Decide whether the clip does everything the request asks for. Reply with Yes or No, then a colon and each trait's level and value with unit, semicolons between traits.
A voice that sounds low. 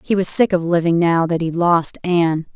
No: medium, 170 Hz